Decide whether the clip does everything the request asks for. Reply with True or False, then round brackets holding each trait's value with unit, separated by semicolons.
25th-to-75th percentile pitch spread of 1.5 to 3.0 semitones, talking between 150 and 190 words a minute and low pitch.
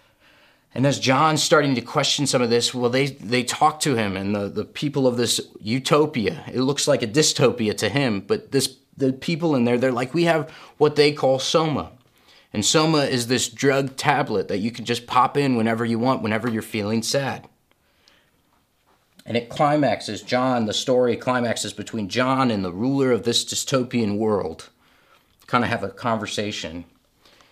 False (3.6 semitones; 180 wpm; 125 Hz)